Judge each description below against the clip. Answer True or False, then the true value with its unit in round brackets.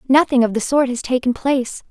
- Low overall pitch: False (255 Hz)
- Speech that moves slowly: False (220 wpm)